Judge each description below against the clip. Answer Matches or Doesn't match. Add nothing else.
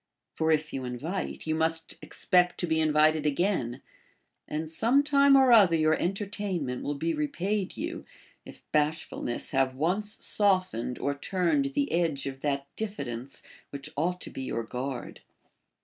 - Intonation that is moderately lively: Doesn't match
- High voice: Doesn't match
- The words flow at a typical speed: Matches